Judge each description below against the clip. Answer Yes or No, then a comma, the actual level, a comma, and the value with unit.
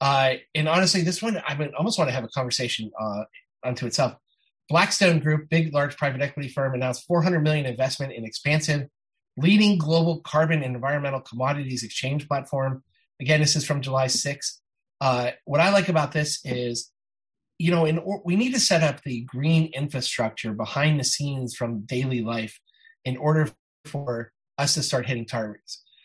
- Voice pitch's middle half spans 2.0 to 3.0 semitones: No, average, 3.5 semitones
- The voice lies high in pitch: No, medium, 140 Hz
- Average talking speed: Yes, average, 170 wpm